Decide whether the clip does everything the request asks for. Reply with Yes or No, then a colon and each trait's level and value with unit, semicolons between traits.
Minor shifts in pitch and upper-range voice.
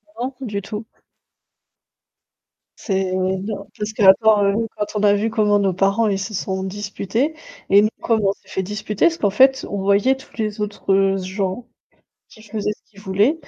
Yes: narrow, 2.0 semitones; high, 205 Hz